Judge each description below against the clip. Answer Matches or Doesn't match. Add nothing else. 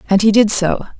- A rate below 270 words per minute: Matches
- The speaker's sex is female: Matches